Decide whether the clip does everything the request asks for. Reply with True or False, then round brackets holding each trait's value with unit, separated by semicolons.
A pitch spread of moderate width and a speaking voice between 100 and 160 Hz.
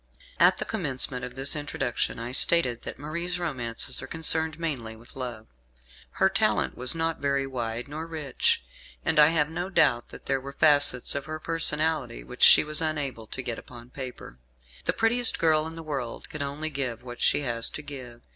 True (4.3 semitones; 140 Hz)